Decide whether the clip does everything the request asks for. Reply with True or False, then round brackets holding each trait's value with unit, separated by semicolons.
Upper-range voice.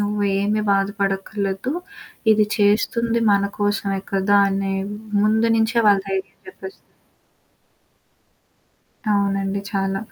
True (200 Hz)